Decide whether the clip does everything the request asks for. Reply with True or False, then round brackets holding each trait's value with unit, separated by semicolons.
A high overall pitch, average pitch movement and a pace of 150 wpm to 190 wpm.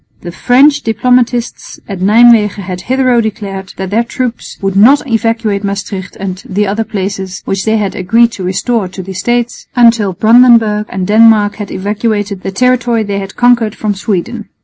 True (215 Hz; 3.3 semitones; 170 wpm)